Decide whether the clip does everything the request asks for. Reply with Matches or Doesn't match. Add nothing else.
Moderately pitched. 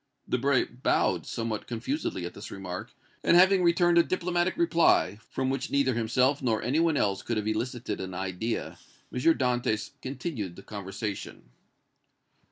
Doesn't match